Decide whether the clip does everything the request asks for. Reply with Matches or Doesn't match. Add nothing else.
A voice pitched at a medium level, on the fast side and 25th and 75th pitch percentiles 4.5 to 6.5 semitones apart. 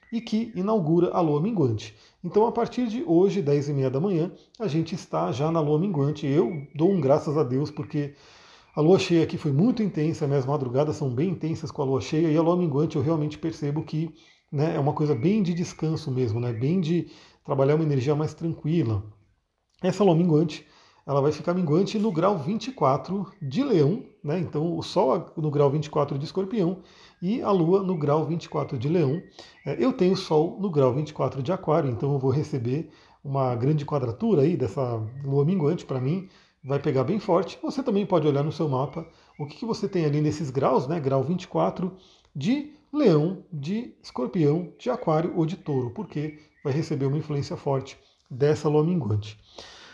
Doesn't match